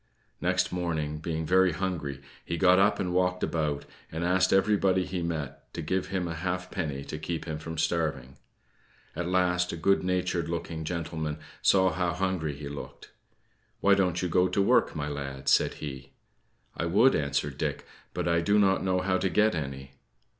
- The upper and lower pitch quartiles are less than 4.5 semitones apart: Yes, average, 3.2 semitones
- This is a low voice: Yes, very low, 85 Hz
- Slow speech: No, average, 180 wpm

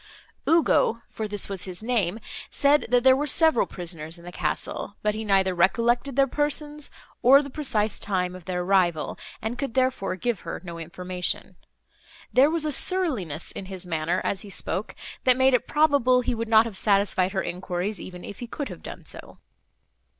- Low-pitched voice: No, high, 215 Hz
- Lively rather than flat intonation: Yes, wide, 6.1 semitones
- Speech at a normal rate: Yes, average, 185 wpm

